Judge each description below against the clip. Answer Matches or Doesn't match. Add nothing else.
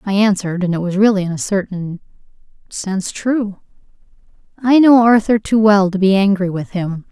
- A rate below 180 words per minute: Matches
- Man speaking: Doesn't match